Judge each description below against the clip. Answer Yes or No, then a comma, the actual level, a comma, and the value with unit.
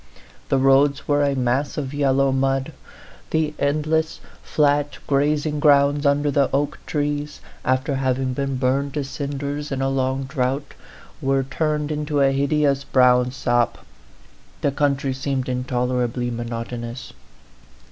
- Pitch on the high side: No, medium, 140 Hz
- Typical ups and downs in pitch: No, narrow, 1.8 semitones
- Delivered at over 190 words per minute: No, slow, 135 wpm